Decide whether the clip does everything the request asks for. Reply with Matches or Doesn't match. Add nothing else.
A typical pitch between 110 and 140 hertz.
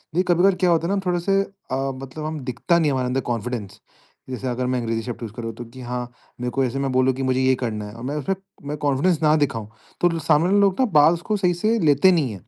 Matches